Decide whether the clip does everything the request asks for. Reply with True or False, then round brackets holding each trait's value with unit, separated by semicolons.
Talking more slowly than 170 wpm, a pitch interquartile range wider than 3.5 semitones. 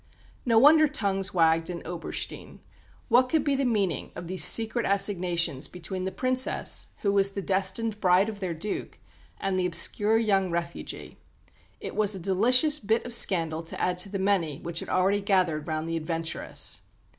False (175 wpm; 4.1 semitones)